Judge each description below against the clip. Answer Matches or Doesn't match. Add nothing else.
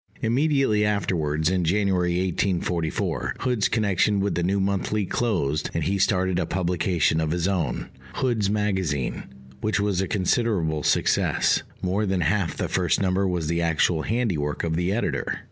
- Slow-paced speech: Doesn't match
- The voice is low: Matches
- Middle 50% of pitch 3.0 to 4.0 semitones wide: Matches